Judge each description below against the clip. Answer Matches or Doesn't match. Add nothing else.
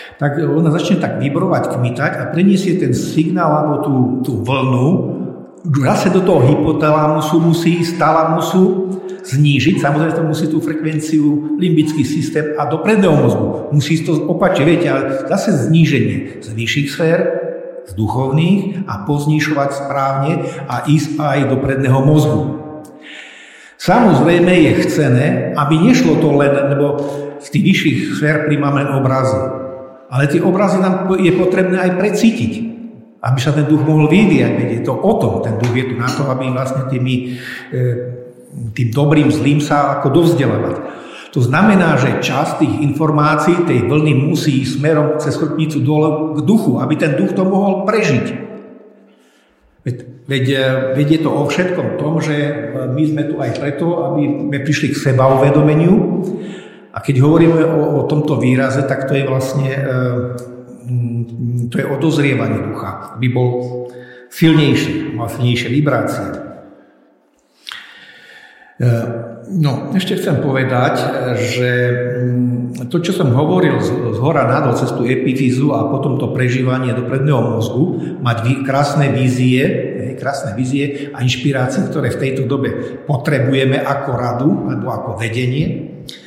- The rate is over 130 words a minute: Matches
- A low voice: Doesn't match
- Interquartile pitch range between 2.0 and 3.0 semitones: Doesn't match